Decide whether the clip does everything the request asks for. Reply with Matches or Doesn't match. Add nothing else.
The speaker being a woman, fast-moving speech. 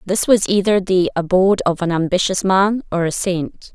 Doesn't match